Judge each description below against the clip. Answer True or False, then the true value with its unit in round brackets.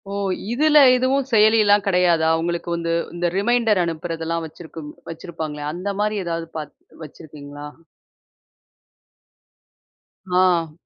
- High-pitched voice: False (170 Hz)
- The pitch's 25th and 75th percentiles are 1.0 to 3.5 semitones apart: False (4.4 semitones)